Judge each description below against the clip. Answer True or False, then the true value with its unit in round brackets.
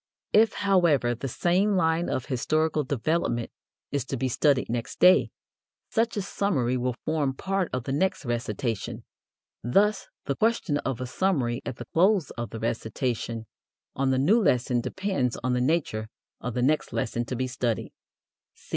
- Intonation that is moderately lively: False (6.6 semitones)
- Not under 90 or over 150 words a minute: False (165 wpm)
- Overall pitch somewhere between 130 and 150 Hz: True (135 Hz)